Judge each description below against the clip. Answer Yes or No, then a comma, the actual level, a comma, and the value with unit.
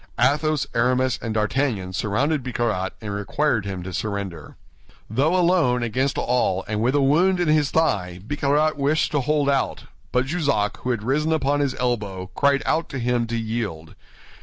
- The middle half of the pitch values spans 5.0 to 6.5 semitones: Yes, wide, 5.4 semitones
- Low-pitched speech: Yes, low, 125 Hz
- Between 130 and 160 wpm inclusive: No, average, 170 wpm